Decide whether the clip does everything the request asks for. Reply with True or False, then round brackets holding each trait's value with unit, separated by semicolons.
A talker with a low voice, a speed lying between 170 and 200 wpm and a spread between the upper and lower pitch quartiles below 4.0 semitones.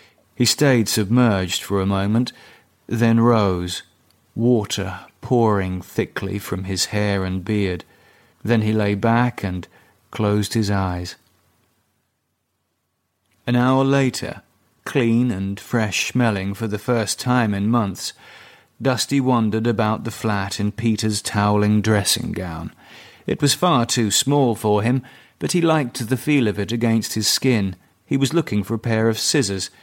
False (110 Hz; 145 wpm; 3.4 semitones)